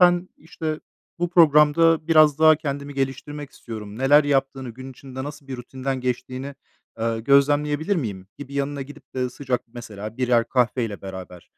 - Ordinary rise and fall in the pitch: Yes, average, 3.2 semitones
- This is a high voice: No, low, 135 Hz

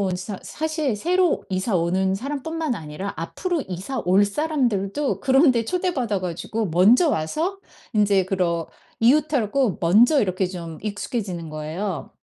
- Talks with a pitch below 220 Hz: Yes, high, 205 Hz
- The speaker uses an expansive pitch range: Yes, wide, 7.3 semitones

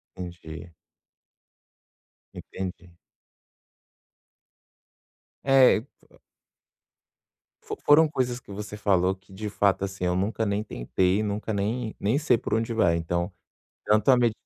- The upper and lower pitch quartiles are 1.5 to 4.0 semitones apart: Yes, average, 3.4 semitones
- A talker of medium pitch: No, low, 100 Hz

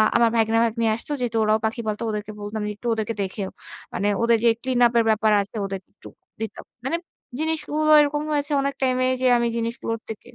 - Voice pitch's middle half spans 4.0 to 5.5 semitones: No, average, 3.1 semitones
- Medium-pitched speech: No, high, 230 Hz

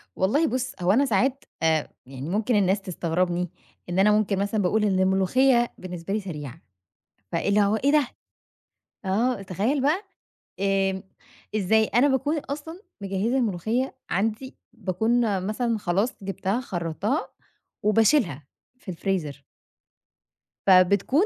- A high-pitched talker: Yes, high, 205 Hz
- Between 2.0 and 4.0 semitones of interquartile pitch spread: No, average, 4.7 semitones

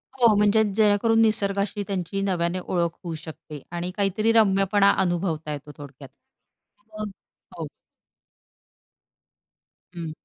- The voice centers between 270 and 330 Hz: No, high, 195 Hz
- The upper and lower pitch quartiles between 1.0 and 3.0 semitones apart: No, average, 3.4 semitones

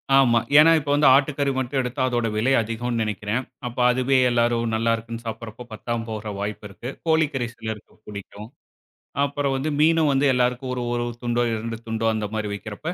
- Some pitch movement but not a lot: Yes, average, 3.3 semitones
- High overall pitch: No, low, 120 Hz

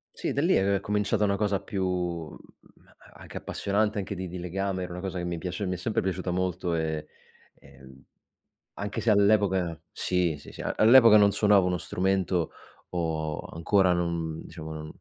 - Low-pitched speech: Yes, very low, 90 Hz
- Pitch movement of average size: Yes, average, 3.0 semitones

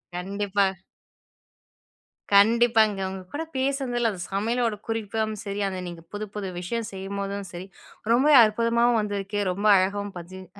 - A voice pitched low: No, high, 205 Hz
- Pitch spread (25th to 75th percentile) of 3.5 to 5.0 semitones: No, average, 3.0 semitones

